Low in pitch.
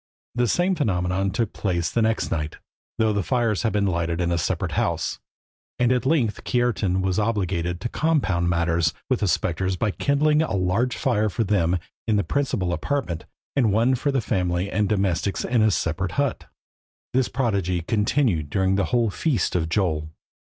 Yes: low, 100 Hz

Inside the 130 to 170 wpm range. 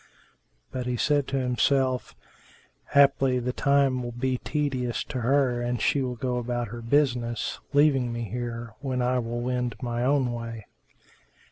Yes: average, 155 wpm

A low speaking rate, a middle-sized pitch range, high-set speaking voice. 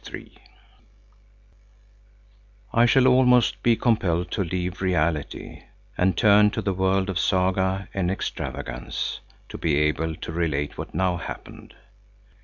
No: slow, 125 wpm; average, 3.2 semitones; very low, 95 Hz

